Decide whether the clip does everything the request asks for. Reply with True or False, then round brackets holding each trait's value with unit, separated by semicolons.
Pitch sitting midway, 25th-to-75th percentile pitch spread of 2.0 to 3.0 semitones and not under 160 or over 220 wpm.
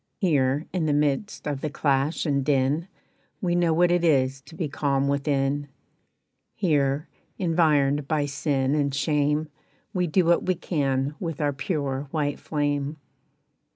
False (145 Hz; 2.7 semitones; 150 wpm)